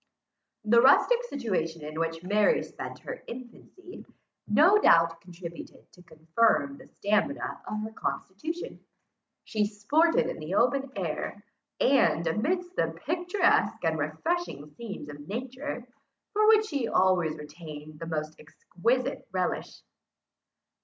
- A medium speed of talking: No, slow, 125 wpm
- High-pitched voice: Yes, high, 210 Hz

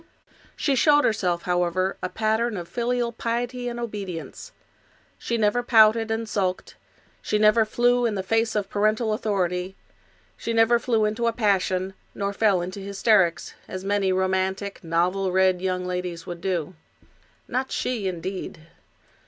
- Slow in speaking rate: No, average, 145 wpm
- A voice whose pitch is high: Yes, high, 200 Hz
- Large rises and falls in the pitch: No, average, 3.6 semitones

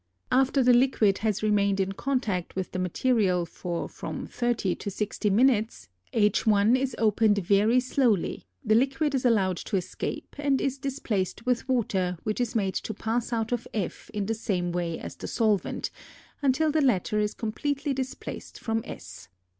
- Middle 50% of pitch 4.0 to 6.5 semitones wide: Yes, average, 4.4 semitones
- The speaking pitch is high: Yes, high, 220 Hz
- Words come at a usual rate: Yes, average, 170 wpm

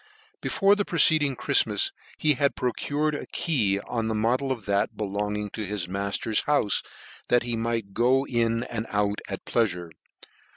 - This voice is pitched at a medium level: No, low, 115 Hz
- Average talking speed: Yes, average, 170 wpm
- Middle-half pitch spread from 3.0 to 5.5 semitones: Yes, average, 4.4 semitones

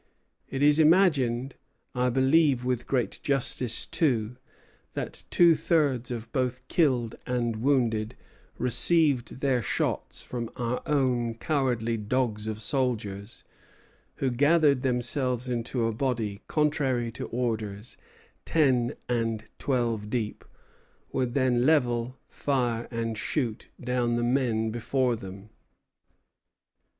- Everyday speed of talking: No, slow, 115 wpm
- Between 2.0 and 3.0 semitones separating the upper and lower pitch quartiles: Yes, narrow, 2.6 semitones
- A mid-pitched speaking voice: No, low, 125 Hz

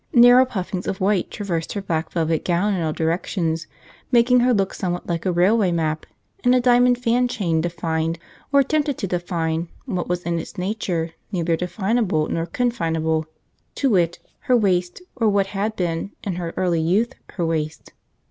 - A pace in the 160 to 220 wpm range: Yes, average, 170 wpm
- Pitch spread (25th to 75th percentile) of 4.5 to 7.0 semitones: Yes, average, 5.1 semitones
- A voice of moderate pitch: Yes, medium, 180 Hz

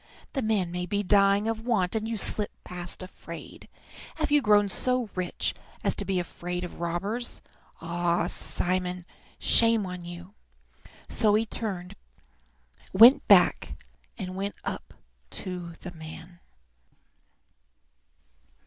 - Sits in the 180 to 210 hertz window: Yes, medium, 185 Hz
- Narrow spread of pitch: No, average, 3.4 semitones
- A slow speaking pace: Yes, slow, 120 wpm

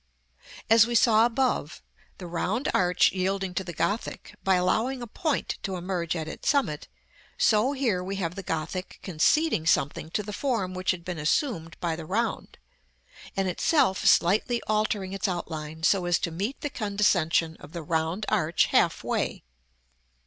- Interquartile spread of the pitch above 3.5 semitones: Yes, average, 4.4 semitones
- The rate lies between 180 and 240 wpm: No, average, 170 wpm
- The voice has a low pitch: No, medium, 185 Hz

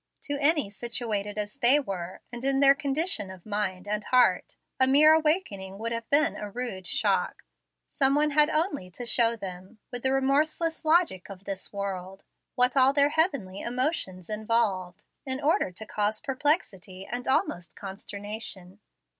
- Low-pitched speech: No, high, 235 Hz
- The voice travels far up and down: Yes, wide, 6.2 semitones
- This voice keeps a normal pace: Yes, average, 160 wpm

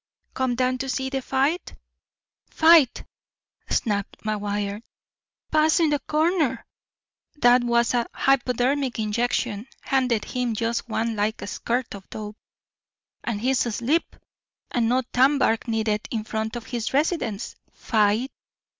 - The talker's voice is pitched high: Yes, high, 245 Hz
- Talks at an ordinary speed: No, slow, 125 wpm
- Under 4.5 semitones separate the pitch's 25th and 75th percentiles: Yes, average, 3.4 semitones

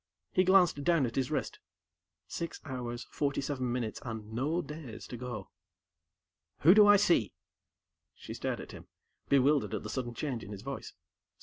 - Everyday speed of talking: Yes, average, 170 wpm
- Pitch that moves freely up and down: No, average, 4.7 semitones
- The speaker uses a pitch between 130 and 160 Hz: Yes, low, 135 Hz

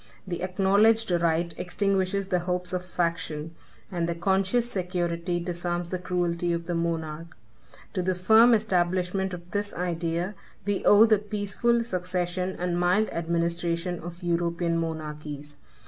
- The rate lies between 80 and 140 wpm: Yes, slow, 135 wpm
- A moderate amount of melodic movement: No, narrow, 2.1 semitones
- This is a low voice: No, medium, 175 Hz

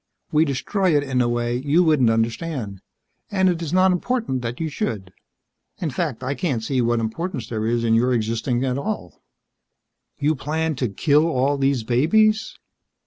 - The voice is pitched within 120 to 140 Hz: Yes, low, 135 Hz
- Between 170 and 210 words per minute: Yes, average, 175 wpm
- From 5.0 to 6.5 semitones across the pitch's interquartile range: Yes, wide, 5.4 semitones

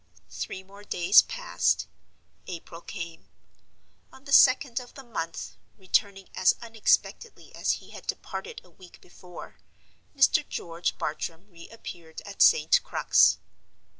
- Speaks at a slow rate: Yes, slow, 120 wpm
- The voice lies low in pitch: No, high, 195 Hz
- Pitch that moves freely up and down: Yes, wide, 7.0 semitones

